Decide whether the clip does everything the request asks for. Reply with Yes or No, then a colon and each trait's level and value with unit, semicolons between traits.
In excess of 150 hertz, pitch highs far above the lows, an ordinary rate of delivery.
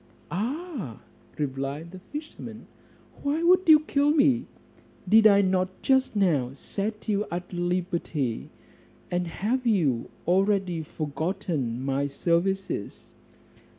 No: medium, 185 Hz; wide, 6.3 semitones; slow, 110 wpm